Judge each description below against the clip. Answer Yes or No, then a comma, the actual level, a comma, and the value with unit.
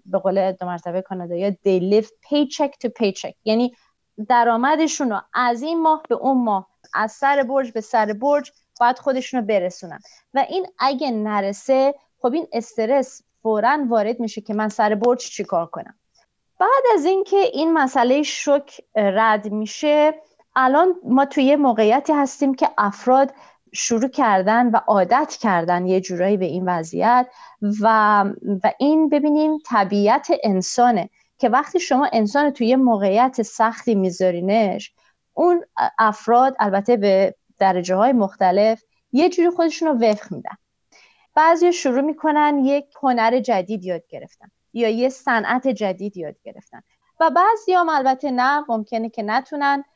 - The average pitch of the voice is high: Yes, high, 245 Hz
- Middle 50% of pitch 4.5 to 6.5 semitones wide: Yes, average, 5.2 semitones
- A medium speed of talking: Yes, average, 145 wpm